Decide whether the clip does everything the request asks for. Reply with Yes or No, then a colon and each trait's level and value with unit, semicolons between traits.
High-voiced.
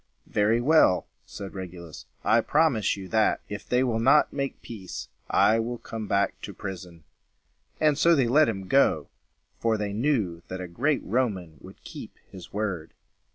No: low, 110 Hz